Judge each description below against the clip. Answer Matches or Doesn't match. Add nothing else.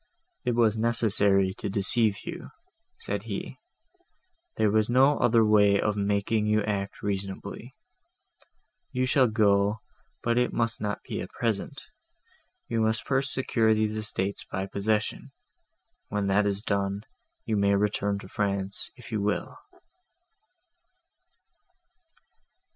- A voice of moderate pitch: Doesn't match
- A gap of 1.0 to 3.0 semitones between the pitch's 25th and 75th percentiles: Matches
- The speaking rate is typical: Doesn't match